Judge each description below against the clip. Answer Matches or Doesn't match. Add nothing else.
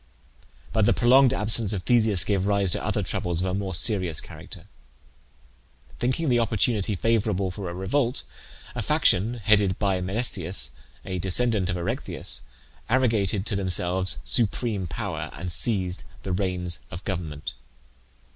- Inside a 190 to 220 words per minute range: Doesn't match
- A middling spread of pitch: Matches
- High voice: Doesn't match